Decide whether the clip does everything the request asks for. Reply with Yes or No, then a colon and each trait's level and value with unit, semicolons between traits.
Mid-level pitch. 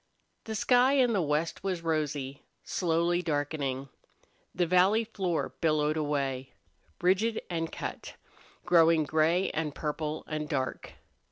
Yes: medium, 160 Hz